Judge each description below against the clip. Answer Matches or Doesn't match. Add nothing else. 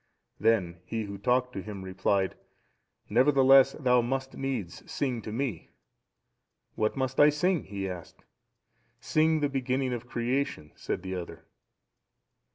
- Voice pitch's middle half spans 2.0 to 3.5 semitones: Doesn't match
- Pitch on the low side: Matches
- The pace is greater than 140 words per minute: Doesn't match